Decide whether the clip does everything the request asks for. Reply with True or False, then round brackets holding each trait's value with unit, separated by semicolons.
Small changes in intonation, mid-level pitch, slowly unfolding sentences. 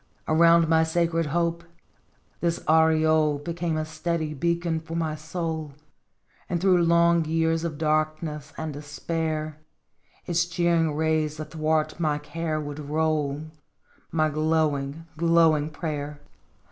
True (1.5 semitones; 160 Hz; 120 wpm)